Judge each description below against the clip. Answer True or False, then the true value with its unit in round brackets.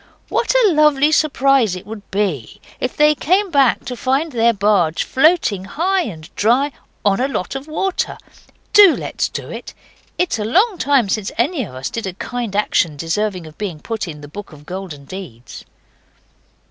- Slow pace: False (180 wpm)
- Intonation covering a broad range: True (7.9 semitones)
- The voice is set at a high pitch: True (225 Hz)